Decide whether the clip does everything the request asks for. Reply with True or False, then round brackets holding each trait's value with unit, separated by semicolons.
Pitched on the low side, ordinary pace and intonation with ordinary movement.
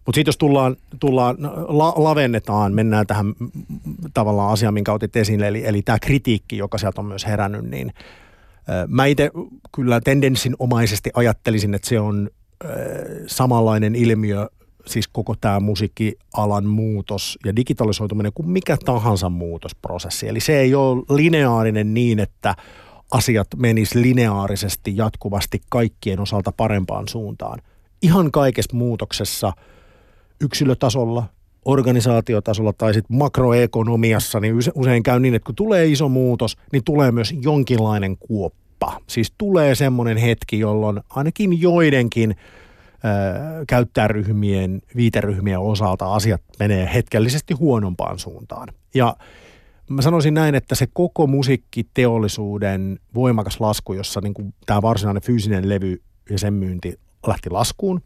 True (110 Hz; 125 wpm; 4.0 semitones)